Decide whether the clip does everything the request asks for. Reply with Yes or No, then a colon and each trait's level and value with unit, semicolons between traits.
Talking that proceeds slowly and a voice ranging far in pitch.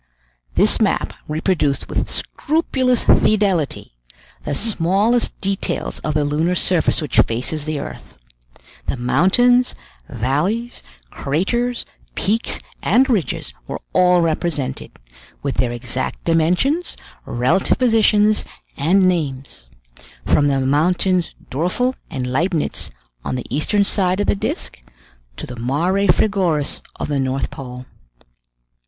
Yes: slow, 115 wpm; wide, 6.6 semitones